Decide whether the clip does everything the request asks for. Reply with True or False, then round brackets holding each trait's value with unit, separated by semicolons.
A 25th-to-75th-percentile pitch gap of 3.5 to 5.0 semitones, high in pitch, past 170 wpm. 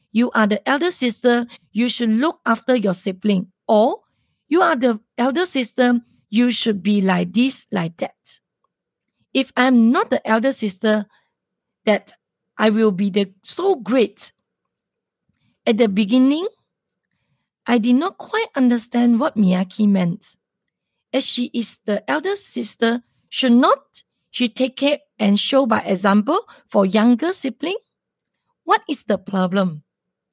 False (4.2 semitones; 235 Hz; 140 wpm)